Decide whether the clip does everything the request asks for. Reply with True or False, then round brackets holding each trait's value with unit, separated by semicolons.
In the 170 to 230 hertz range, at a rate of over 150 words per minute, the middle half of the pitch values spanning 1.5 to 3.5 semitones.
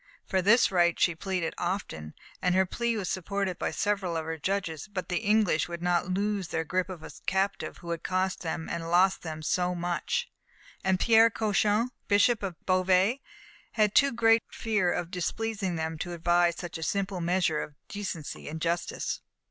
True (185 Hz; 180 wpm; 3.0 semitones)